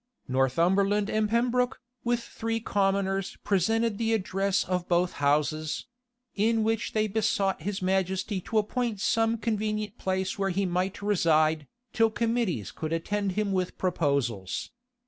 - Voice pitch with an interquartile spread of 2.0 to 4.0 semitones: Yes, average, 3.4 semitones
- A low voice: No, high, 195 Hz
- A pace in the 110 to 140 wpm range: Yes, slow, 135 wpm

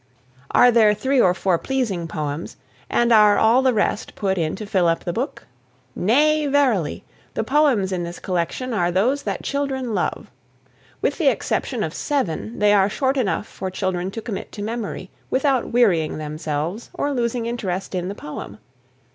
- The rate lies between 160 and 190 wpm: Yes, average, 170 wpm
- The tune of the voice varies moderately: No, wide, 5.8 semitones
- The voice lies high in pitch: Yes, high, 210 Hz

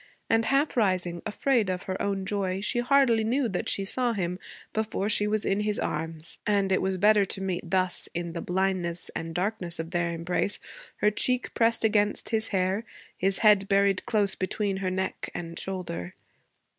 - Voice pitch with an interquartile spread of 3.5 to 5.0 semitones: No, average, 2.8 semitones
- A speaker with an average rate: Yes, average, 180 wpm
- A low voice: No, high, 195 Hz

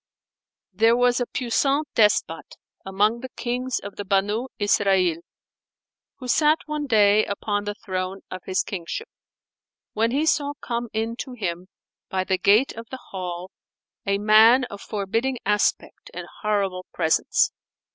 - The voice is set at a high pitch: Yes, high, 210 Hz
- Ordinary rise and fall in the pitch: Yes, average, 4.2 semitones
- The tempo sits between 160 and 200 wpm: No, average, 145 wpm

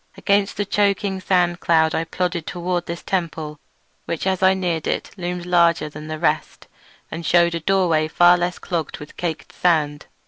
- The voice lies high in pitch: No, medium, 175 Hz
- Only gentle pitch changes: Yes, narrow, 2.2 semitones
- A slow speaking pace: No, average, 175 wpm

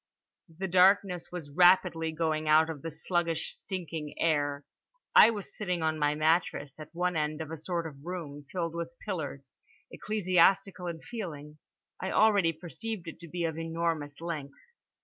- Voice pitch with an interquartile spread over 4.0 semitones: No, average, 2.7 semitones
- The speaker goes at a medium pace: Yes, average, 160 wpm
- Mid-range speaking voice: Yes, medium, 165 Hz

